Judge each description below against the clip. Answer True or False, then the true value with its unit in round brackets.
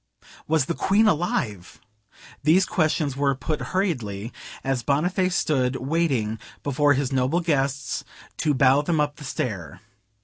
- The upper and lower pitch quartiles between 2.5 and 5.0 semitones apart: True (4.0 semitones)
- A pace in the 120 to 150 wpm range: True (135 wpm)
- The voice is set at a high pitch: False (140 Hz)